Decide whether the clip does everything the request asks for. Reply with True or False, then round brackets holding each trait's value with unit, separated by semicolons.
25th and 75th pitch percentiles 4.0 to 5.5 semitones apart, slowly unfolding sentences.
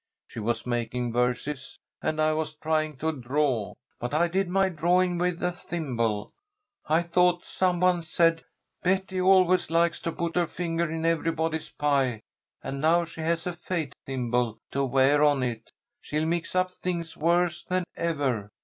False (4.3 semitones; 165 wpm)